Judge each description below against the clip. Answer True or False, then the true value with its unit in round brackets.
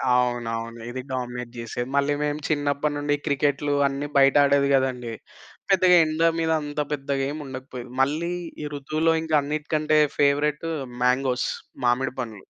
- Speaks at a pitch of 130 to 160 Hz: True (140 Hz)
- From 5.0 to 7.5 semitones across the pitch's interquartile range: False (3.0 semitones)